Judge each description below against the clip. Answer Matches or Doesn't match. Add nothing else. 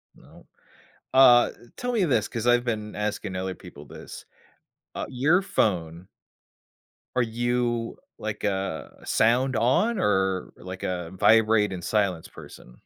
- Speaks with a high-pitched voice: Doesn't match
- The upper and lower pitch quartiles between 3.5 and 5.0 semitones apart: Matches